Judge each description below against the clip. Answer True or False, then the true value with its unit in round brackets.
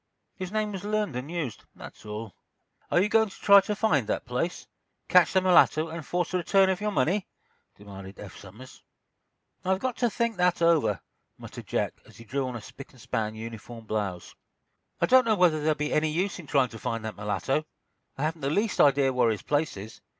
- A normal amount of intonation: False (8.4 semitones)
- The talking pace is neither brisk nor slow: False (210 wpm)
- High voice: False (155 Hz)